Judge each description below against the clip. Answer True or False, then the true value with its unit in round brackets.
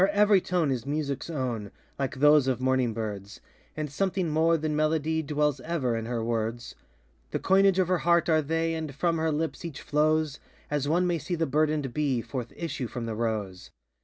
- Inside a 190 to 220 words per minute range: True (195 wpm)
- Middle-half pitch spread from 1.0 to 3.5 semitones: False (4.4 semitones)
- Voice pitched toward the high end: False (150 Hz)